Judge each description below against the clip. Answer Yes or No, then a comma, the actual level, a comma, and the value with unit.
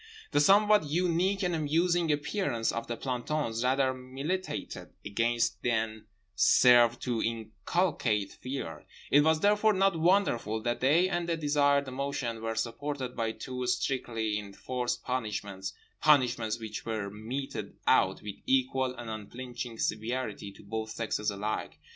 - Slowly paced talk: Yes, slow, 130 wpm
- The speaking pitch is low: Yes, low, 125 Hz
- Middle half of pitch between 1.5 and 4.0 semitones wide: No, average, 4.8 semitones